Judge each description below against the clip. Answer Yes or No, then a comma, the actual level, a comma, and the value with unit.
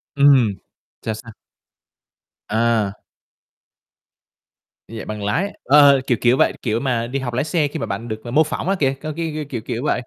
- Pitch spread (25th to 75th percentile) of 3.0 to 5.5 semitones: Yes, average, 4.2 semitones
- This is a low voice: Yes, low, 125 Hz